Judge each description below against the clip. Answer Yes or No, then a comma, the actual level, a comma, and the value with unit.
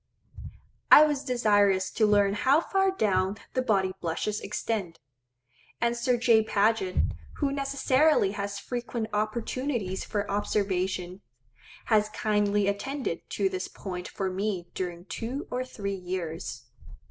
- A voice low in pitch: No, high, 210 Hz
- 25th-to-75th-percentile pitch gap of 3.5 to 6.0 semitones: Yes, average, 4.1 semitones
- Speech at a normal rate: No, slow, 125 wpm